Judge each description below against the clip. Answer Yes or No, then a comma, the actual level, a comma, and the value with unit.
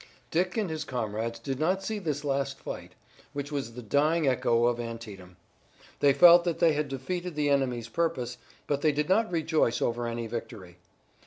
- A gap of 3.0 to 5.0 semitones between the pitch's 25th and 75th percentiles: No, wide, 5.4 semitones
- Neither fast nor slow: Yes, average, 180 wpm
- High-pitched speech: No, medium, 140 Hz